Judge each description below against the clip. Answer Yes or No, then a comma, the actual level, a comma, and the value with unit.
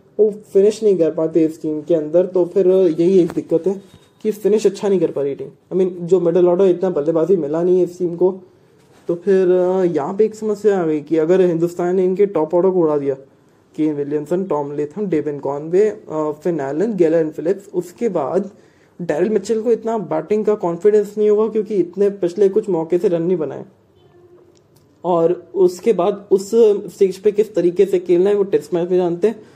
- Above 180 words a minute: Yes, average, 195 wpm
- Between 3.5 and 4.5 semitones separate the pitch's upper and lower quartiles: Yes, average, 3.8 semitones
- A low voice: No, medium, 180 Hz